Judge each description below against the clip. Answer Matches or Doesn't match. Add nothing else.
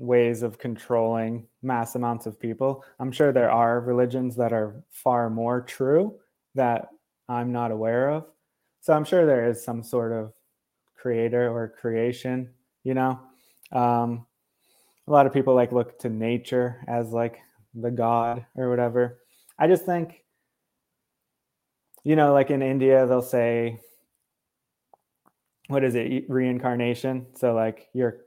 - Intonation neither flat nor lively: Doesn't match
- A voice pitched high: Doesn't match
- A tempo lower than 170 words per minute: Matches